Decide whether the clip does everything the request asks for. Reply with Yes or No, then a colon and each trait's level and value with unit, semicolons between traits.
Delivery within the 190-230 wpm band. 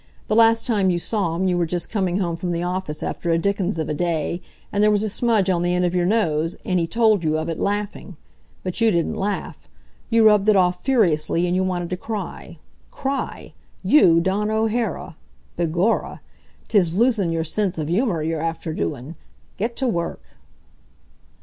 Yes: average, 195 wpm